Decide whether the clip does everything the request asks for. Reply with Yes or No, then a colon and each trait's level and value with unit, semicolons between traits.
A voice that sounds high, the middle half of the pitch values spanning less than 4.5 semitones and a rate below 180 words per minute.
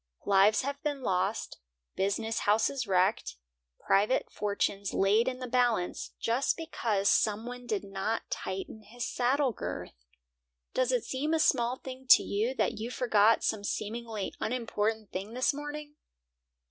Yes: high, 225 Hz; average, 3.8 semitones; average, 145 wpm